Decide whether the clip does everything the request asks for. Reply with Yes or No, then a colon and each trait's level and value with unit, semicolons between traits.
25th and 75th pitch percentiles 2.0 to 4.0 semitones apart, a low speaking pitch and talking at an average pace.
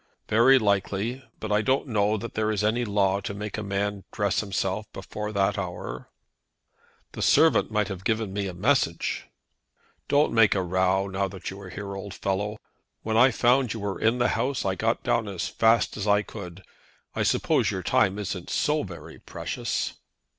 Yes: narrow, 2.4 semitones; low, 105 Hz; average, 185 wpm